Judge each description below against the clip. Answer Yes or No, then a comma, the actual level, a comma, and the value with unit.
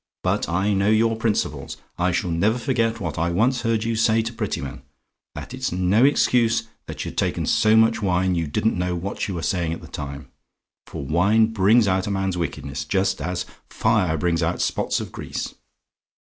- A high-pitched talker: No, very low, 95 Hz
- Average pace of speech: Yes, average, 190 wpm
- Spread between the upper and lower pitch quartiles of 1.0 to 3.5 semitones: No, average, 4.3 semitones